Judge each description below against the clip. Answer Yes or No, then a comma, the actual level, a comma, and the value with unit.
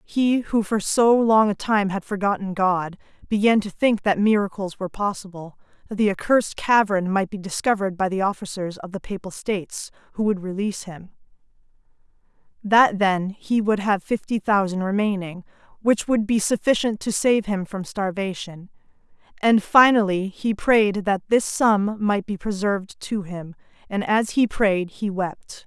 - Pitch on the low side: No, high, 200 Hz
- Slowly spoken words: No, average, 160 wpm